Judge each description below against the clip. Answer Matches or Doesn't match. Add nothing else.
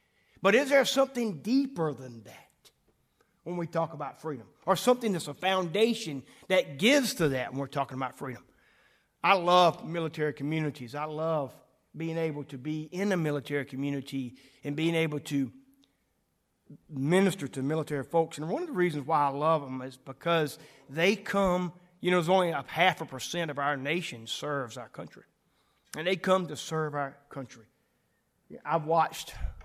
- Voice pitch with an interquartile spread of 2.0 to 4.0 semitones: Doesn't match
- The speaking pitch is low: Doesn't match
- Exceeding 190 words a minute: Doesn't match